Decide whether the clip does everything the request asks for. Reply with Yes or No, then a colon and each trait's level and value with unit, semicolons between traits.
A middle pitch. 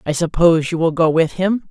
Yes: medium, 165 Hz